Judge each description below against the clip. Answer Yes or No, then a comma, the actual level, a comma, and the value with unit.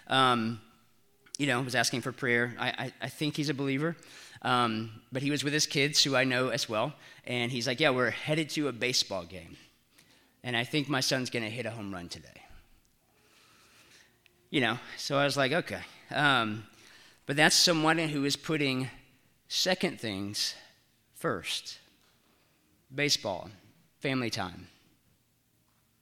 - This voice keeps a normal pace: Yes, average, 155 wpm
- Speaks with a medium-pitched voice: No, low, 130 Hz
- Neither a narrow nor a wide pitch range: Yes, average, 3.7 semitones